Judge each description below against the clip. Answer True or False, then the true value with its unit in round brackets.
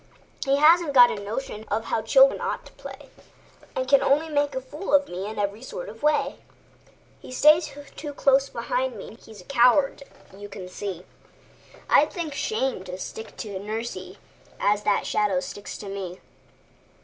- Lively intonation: True (6.0 semitones)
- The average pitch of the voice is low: False (250 Hz)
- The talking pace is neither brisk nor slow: True (160 wpm)